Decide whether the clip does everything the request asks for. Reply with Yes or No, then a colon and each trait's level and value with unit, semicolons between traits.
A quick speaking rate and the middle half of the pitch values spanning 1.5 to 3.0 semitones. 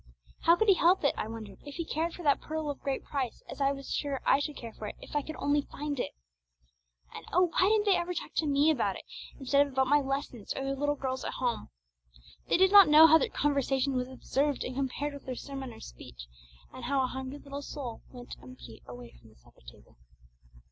Yes: fast, 240 wpm; average, 2.7 semitones